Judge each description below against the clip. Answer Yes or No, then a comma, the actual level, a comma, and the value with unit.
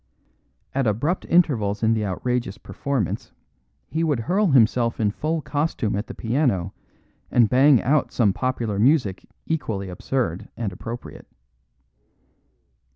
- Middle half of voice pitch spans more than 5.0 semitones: Yes, wide, 5.5 semitones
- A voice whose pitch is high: No, low, 120 Hz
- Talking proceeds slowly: Yes, slow, 125 wpm